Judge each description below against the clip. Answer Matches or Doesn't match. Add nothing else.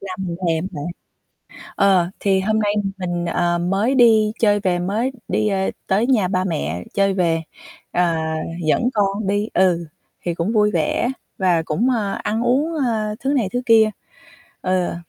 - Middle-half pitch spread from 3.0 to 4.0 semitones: Matches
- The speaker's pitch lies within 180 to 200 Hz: Matches